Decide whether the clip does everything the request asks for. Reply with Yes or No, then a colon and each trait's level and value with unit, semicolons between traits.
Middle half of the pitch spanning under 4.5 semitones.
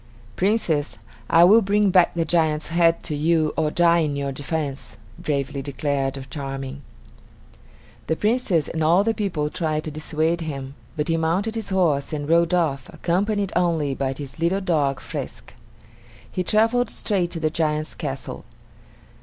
Yes: average, 3.6 semitones